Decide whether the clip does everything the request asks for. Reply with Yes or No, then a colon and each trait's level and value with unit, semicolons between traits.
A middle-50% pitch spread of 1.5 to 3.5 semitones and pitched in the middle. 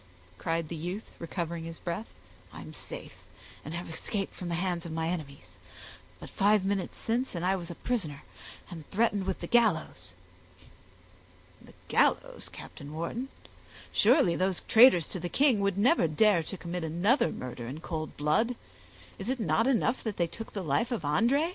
No: average, 5.2 semitones; medium, 180 Hz